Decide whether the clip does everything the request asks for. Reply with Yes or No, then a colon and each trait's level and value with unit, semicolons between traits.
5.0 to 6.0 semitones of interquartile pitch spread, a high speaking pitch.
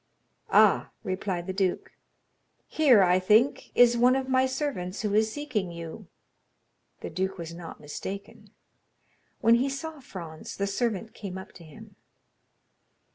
Yes: wide, 5.4 semitones; high, 200 Hz